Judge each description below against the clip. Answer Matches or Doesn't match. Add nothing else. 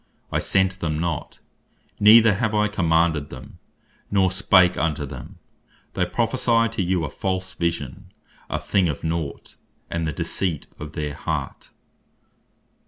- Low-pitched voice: Matches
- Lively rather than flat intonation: Doesn't match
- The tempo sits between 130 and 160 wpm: Matches